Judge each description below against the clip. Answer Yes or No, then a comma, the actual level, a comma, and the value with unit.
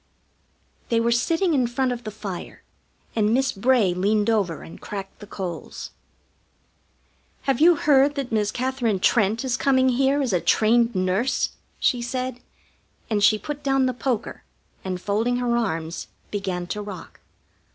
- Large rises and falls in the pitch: No, average, 4.3 semitones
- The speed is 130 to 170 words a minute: Yes, average, 155 wpm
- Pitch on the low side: No, high, 235 Hz